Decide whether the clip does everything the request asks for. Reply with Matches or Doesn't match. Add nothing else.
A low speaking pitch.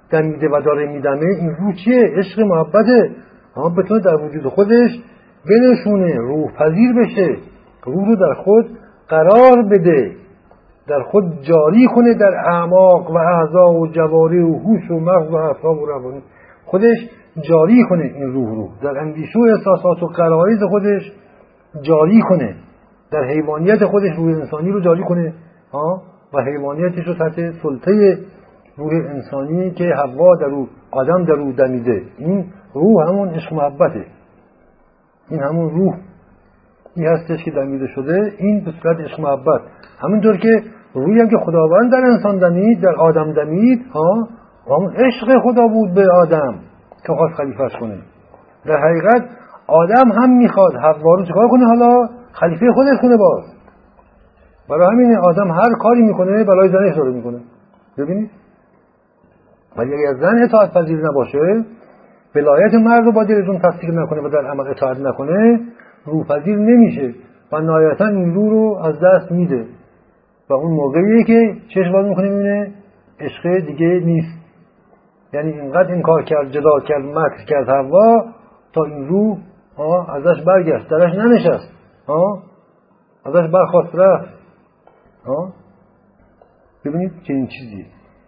Doesn't match